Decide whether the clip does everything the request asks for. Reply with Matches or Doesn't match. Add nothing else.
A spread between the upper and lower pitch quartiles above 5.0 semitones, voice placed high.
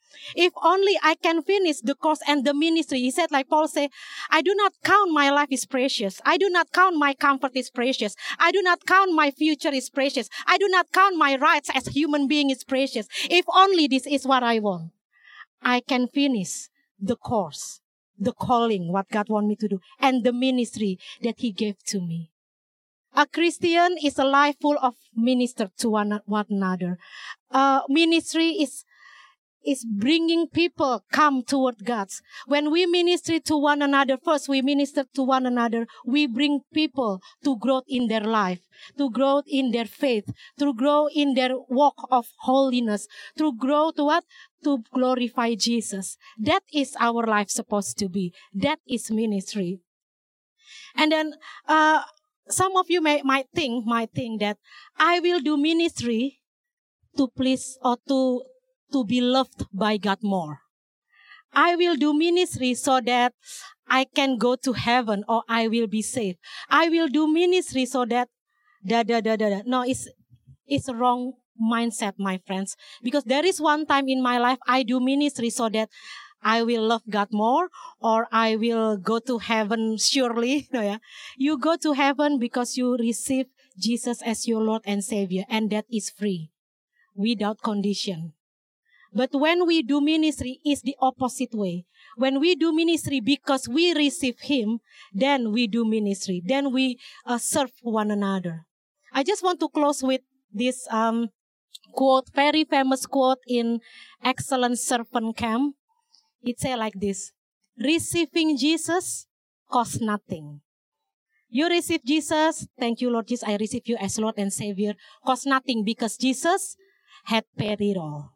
Doesn't match